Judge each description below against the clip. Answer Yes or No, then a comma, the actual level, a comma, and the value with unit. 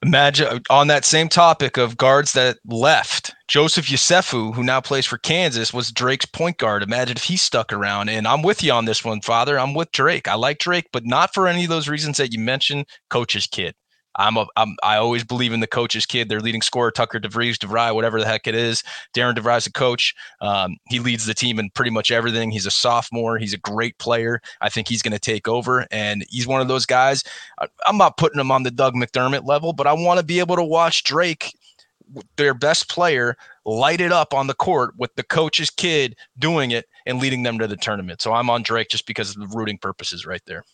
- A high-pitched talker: No, low, 120 Hz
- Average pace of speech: No, fast, 235 wpm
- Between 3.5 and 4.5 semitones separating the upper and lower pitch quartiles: Yes, average, 3.9 semitones